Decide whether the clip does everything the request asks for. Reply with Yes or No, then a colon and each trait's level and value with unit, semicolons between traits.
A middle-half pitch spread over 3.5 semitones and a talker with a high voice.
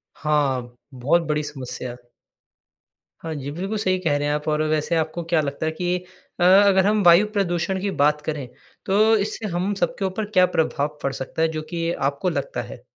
No: average, 4.3 semitones; medium, 165 Hz